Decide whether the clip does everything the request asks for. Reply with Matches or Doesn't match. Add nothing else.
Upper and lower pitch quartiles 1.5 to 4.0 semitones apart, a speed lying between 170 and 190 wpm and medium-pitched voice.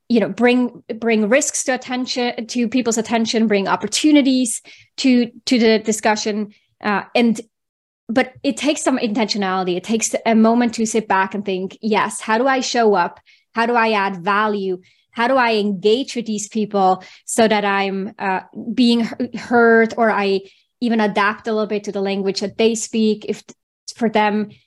Doesn't match